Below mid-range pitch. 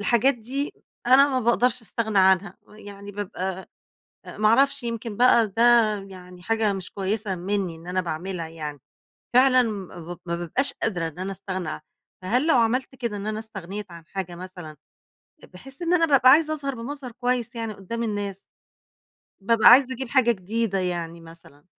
No: high, 210 Hz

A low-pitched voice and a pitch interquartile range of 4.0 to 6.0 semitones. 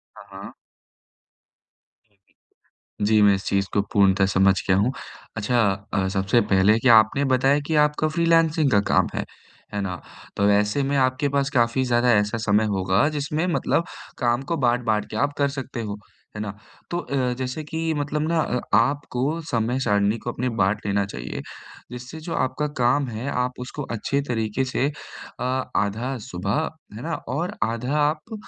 Yes: low, 125 Hz; wide, 5.4 semitones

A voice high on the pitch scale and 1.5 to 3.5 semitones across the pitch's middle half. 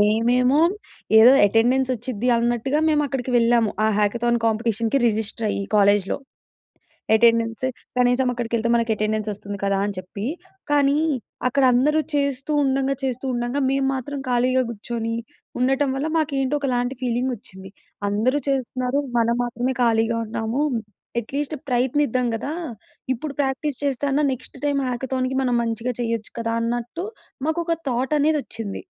Yes: high, 245 Hz; average, 2.9 semitones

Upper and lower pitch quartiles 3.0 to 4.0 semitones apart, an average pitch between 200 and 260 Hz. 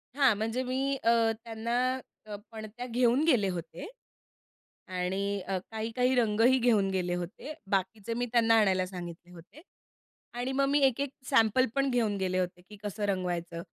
No: average, 4.6 semitones; high, 220 Hz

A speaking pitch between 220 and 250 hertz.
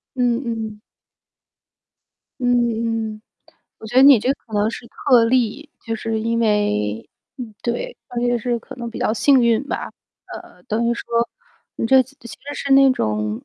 Yes: high, 235 Hz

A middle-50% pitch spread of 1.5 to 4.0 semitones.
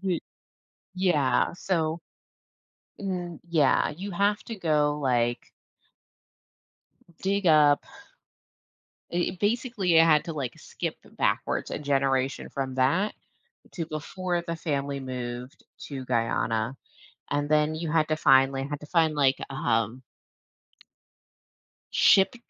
No: average, 4.5 semitones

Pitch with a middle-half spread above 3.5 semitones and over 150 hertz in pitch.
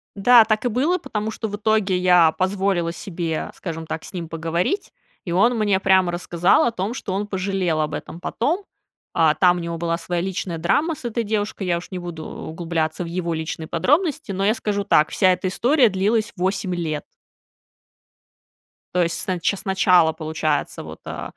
Yes: average, 3.9 semitones; medium, 185 Hz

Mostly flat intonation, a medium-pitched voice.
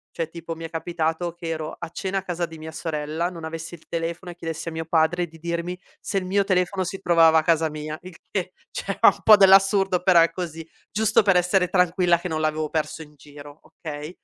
Yes: narrow, 2.2 semitones; medium, 170 Hz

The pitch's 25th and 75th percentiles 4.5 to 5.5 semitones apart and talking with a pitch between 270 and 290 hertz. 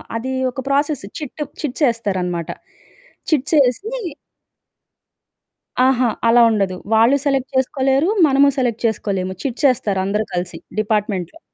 No: average, 5.0 semitones; high, 245 Hz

